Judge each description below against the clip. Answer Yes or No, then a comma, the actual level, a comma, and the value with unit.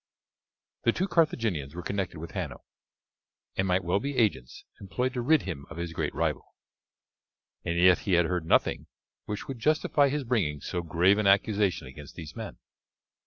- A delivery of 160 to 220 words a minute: Yes, average, 170 wpm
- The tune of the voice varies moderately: No, wide, 5.8 semitones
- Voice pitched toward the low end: Yes, very low, 95 Hz